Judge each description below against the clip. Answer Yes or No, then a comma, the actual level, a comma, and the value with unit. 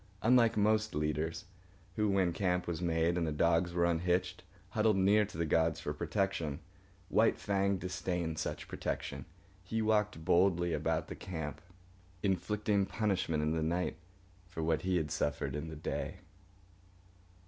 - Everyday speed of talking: Yes, average, 150 wpm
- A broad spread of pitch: No, average, 3.4 semitones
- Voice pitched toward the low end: Yes, very low, 90 Hz